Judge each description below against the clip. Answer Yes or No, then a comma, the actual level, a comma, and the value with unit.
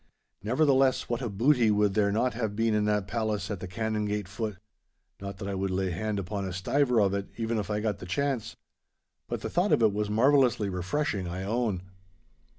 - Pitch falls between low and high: No, low, 105 Hz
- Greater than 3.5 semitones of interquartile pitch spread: No, average, 2.9 semitones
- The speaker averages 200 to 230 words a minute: Yes, fast, 205 wpm